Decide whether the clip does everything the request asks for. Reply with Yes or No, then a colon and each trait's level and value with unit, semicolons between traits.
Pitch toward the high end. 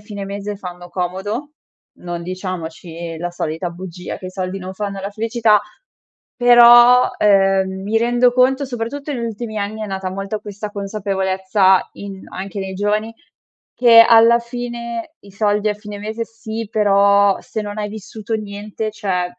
Yes: high, 205 Hz